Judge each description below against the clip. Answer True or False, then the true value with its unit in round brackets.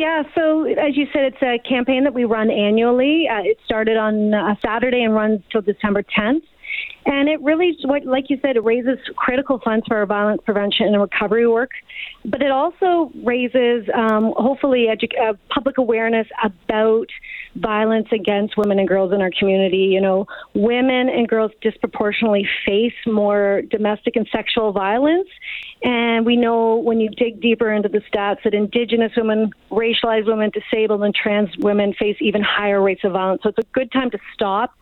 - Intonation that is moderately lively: True (3.6 semitones)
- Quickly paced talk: False (180 wpm)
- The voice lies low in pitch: False (225 Hz)